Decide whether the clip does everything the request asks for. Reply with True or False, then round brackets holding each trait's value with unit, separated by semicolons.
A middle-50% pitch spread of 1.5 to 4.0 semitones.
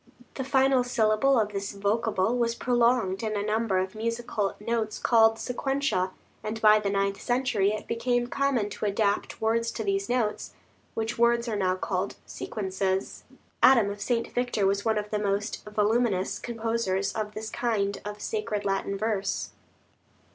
True (2.7 semitones)